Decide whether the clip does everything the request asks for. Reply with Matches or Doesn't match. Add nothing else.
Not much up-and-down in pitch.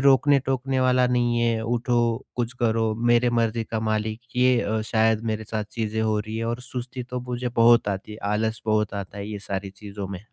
Matches